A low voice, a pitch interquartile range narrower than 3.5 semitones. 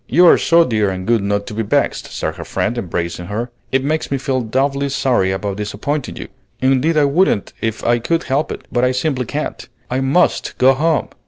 No: low, 125 Hz; average, 4.8 semitones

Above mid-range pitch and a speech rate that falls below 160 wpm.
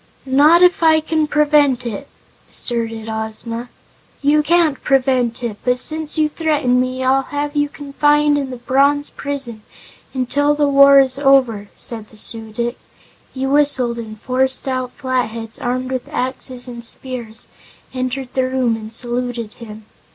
Yes: very high, 260 Hz; average, 150 wpm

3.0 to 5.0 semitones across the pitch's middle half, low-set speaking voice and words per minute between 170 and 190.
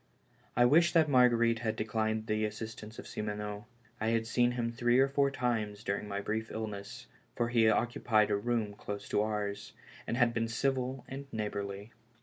No: narrow, 2.5 semitones; low, 110 Hz; average, 180 wpm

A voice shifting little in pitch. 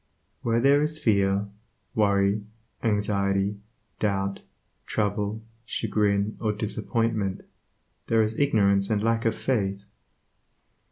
Yes: narrow, 2.2 semitones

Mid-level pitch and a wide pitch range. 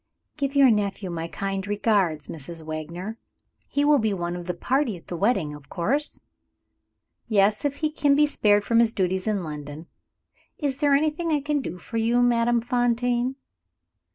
No: high, 220 Hz; wide, 7.2 semitones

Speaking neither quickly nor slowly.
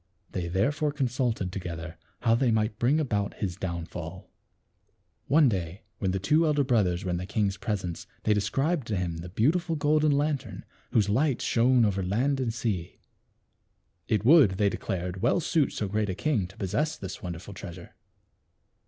Yes: average, 170 wpm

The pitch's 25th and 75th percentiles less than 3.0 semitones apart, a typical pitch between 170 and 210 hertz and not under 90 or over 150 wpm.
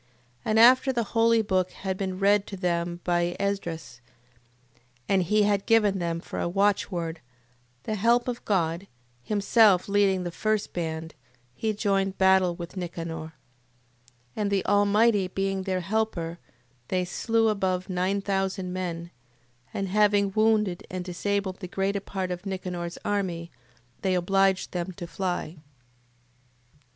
Yes: narrow, 2.6 semitones; high, 190 Hz; average, 140 wpm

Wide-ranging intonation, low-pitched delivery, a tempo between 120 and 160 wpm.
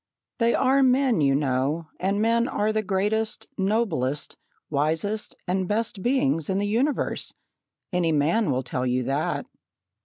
No: wide, 7.2 semitones; high, 190 Hz; average, 145 wpm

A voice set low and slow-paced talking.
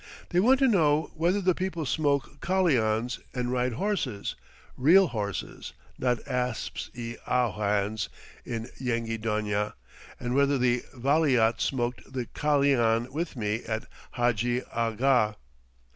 Yes: low, 125 Hz; slow, 125 wpm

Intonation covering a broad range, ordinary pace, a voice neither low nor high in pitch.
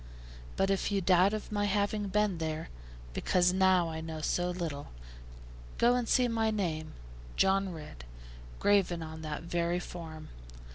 No: average, 3.9 semitones; average, 150 wpm; medium, 180 Hz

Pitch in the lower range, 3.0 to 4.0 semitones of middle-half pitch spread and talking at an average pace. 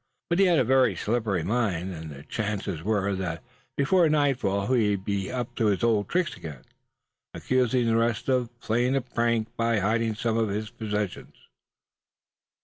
Yes: low, 110 Hz; average, 3.5 semitones; average, 170 wpm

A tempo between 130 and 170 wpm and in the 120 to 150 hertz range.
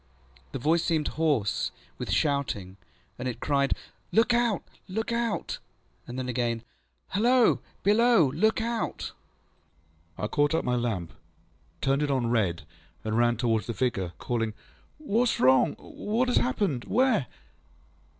Yes: average, 140 wpm; medium, 140 Hz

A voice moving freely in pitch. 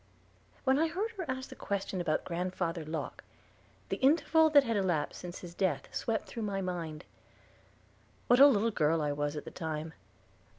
Yes: wide, 8.4 semitones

